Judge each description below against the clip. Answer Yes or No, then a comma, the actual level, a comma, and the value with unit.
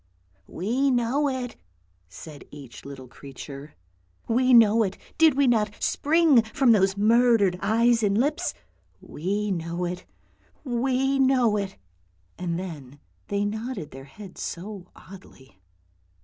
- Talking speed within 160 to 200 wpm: No, slow, 135 wpm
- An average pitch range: No, wide, 6.5 semitones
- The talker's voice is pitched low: No, high, 205 Hz